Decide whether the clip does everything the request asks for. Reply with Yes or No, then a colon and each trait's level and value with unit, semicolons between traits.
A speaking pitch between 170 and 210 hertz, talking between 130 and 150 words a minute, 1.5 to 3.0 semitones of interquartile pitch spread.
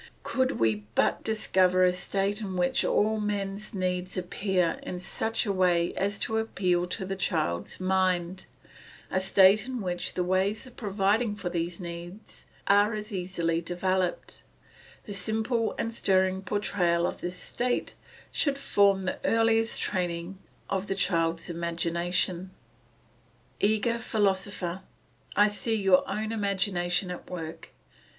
Yes: high, 190 Hz; slow, 135 wpm; average, 2.7 semitones